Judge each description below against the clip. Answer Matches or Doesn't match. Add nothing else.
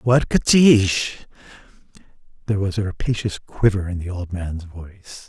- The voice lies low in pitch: Matches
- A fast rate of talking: Doesn't match